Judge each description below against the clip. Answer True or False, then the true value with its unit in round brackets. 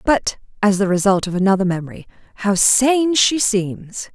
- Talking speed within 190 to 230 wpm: False (160 wpm)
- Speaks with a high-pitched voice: True (205 Hz)